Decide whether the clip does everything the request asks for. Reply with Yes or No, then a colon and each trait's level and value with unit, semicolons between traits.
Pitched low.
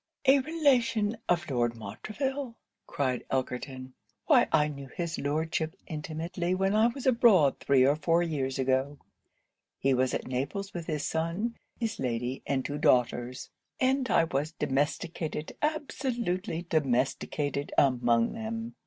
No: medium, 155 Hz